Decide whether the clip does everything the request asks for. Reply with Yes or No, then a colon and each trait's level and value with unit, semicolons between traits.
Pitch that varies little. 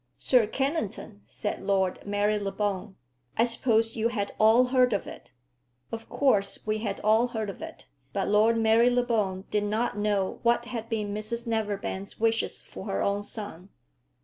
Yes: narrow, 2.3 semitones